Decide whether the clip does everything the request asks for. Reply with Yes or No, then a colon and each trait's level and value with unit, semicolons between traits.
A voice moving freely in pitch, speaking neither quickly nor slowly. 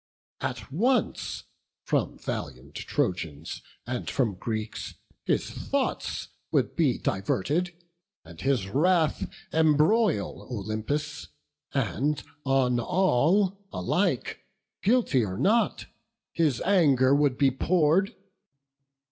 No: wide, 7.6 semitones; slow, 95 wpm